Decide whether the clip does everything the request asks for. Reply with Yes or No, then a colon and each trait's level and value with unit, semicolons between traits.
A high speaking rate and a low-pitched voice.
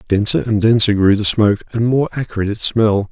Yes: fast, 210 wpm; low, 110 Hz